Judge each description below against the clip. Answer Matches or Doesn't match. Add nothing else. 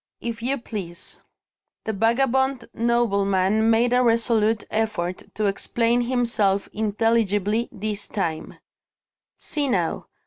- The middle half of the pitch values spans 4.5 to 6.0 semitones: Doesn't match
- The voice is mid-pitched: Doesn't match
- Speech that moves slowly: Matches